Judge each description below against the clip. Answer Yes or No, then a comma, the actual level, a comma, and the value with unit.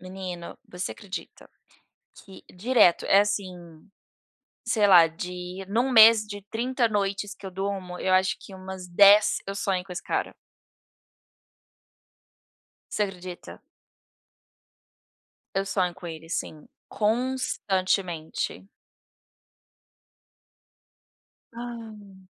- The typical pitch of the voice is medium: No, high, 195 Hz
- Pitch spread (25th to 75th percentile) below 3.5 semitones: Yes, narrow, 2.5 semitones